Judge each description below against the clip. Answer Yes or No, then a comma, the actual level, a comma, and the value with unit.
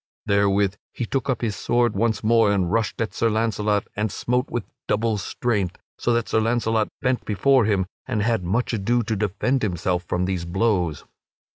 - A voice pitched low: Yes, low, 110 Hz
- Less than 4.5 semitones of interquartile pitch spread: Yes, average, 3.0 semitones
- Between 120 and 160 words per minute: No, average, 180 wpm